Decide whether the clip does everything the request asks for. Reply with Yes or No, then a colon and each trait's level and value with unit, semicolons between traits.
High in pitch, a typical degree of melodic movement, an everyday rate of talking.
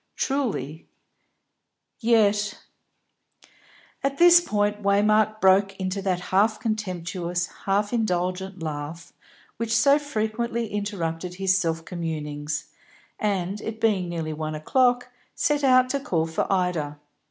No: high, 195 Hz; average, 4.4 semitones; slow, 115 wpm